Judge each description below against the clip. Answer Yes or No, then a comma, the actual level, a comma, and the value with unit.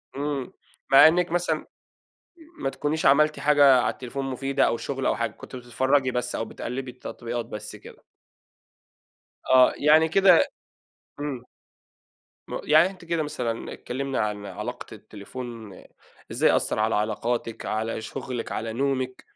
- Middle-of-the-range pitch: No, low, 130 Hz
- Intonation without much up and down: No, average, 4.2 semitones